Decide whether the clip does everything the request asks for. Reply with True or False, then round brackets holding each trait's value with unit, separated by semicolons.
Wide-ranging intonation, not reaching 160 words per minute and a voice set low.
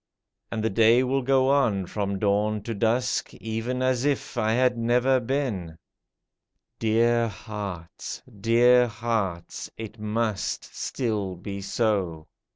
False (3.2 semitones; 140 wpm; 115 Hz)